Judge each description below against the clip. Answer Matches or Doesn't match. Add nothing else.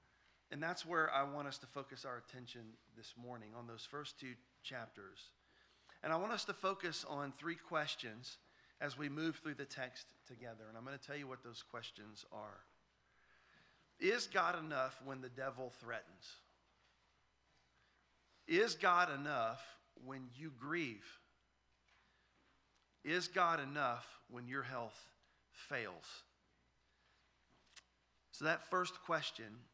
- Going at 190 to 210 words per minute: Doesn't match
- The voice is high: Doesn't match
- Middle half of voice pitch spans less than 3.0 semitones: Doesn't match